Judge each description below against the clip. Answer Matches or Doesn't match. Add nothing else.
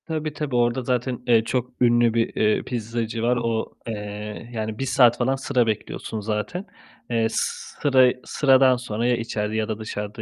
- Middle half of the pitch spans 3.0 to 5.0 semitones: Doesn't match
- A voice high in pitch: Doesn't match